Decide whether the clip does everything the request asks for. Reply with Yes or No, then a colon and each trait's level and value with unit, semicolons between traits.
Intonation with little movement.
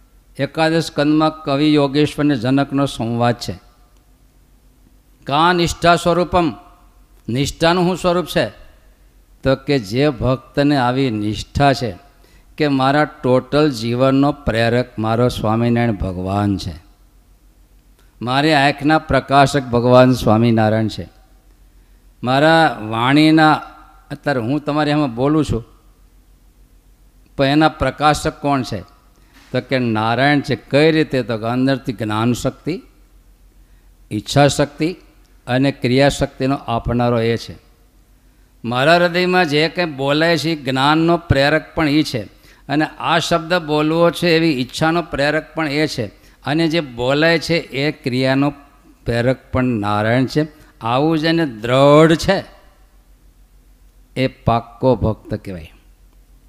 No: average, 4.5 semitones